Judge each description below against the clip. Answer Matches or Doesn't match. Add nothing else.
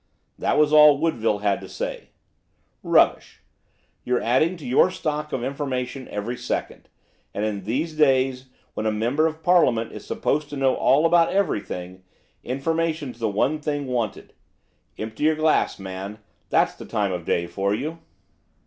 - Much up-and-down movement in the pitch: Matches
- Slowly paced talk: Doesn't match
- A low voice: Matches